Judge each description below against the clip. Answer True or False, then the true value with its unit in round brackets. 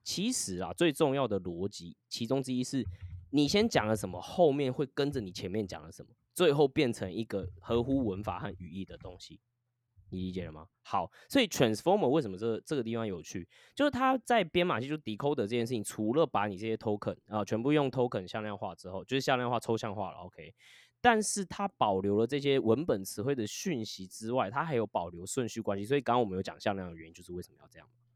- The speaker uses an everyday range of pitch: False (6.1 semitones)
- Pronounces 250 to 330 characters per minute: False (385 characters per minute)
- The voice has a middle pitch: False (115 Hz)